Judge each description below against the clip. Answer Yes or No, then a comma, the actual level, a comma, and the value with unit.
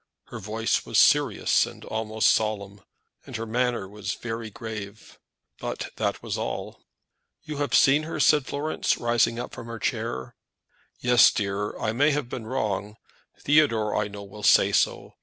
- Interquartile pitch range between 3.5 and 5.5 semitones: No, average, 3.0 semitones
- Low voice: Yes, low, 110 Hz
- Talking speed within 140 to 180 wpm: Yes, average, 160 wpm